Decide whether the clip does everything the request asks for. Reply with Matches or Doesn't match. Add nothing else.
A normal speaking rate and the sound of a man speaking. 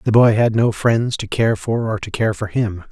Doesn't match